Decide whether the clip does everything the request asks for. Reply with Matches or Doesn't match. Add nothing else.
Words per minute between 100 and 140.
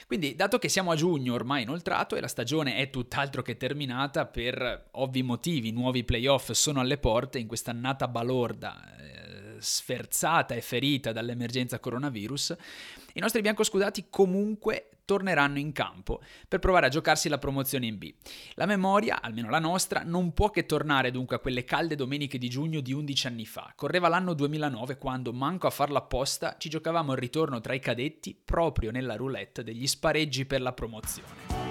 Doesn't match